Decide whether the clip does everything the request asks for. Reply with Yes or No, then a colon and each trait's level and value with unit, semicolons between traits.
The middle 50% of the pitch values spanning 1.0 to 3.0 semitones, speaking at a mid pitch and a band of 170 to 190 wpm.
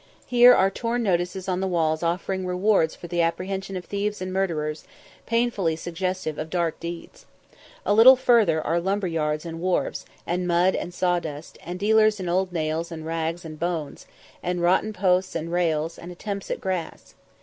Yes: narrow, 2.6 semitones; medium, 180 Hz; average, 175 wpm